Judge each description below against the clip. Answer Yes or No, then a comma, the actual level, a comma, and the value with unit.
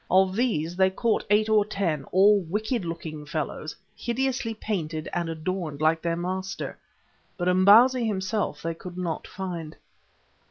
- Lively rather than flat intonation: No, average, 4.3 semitones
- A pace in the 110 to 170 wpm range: Yes, average, 145 wpm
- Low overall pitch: No, medium, 185 Hz